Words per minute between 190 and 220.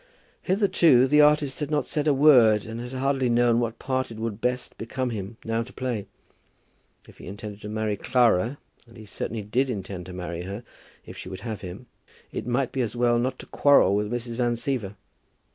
Yes: fast, 205 wpm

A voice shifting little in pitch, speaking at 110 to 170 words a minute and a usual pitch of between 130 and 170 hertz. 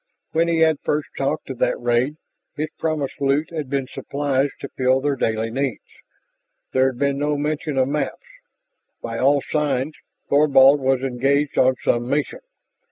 Yes: narrow, 2.2 semitones; average, 165 wpm; medium, 140 Hz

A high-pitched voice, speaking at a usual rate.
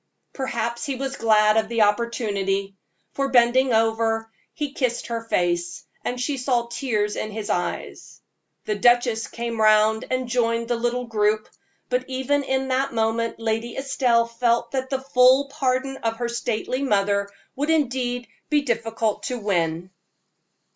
Yes: high, 235 Hz; average, 150 wpm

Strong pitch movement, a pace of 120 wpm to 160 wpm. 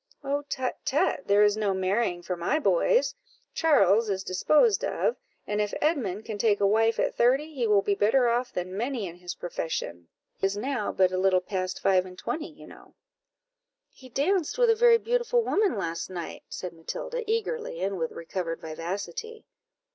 No: wide, 8.5 semitones; average, 185 wpm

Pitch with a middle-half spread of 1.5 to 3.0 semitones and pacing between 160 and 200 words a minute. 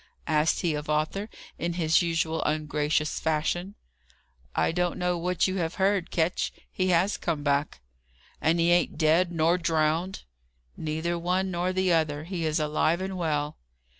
Yes: narrow, 2.5 semitones; average, 165 wpm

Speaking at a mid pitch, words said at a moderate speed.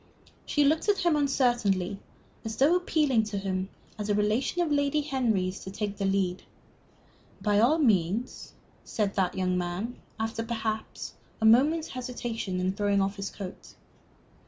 No: high, 220 Hz; average, 155 wpm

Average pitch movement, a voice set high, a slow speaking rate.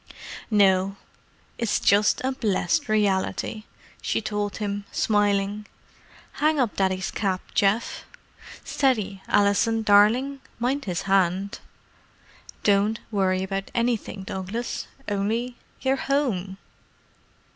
Yes: average, 3.1 semitones; high, 205 Hz; slow, 90 wpm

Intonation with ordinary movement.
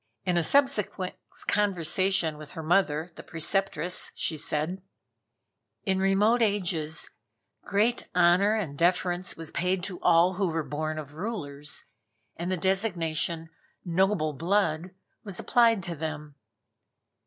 Yes: average, 3.4 semitones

